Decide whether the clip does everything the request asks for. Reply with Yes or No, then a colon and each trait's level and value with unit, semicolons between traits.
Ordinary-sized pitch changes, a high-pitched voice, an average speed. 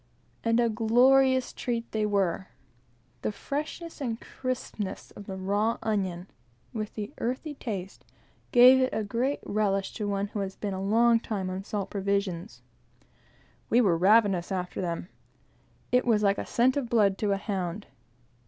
Yes: average, 3.5 semitones; high, 210 Hz; average, 160 wpm